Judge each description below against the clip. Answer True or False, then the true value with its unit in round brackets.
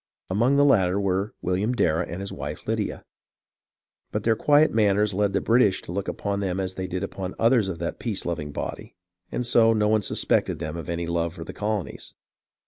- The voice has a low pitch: True (100 Hz)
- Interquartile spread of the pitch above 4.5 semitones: False (3.3 semitones)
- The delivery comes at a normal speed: False (210 wpm)